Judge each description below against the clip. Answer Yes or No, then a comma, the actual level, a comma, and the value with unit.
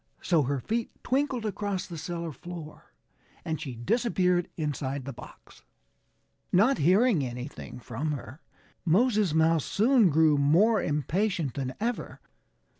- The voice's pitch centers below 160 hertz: No, medium, 165 Hz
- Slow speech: Yes, slow, 125 wpm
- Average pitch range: No, wide, 6.5 semitones